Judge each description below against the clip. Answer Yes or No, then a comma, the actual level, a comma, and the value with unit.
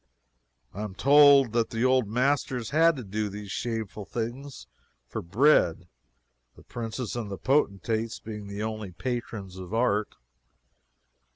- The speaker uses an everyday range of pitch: Yes, average, 3.8 semitones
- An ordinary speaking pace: No, slow, 130 wpm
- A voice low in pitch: Yes, low, 115 Hz